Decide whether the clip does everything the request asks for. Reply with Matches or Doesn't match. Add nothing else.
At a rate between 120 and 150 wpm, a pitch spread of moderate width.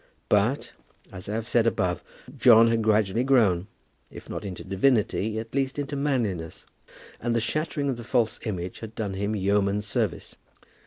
Doesn't match